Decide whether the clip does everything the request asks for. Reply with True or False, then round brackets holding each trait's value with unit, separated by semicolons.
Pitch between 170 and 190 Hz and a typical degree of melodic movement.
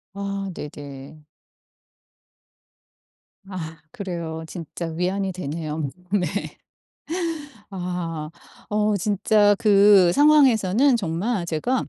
True (185 Hz; 4.2 semitones)